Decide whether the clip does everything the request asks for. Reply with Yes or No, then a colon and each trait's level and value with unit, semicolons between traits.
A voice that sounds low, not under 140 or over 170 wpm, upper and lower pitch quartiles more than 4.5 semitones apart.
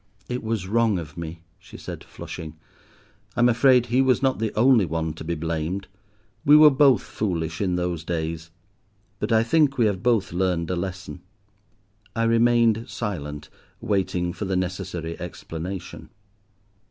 Yes: very low, 95 Hz; average, 155 wpm; wide, 5.5 semitones